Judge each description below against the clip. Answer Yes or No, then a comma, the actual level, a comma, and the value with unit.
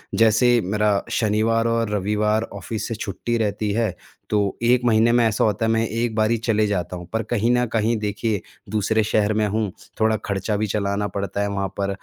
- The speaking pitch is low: Yes, low, 110 Hz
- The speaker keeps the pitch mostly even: Yes, narrow, 1.8 semitones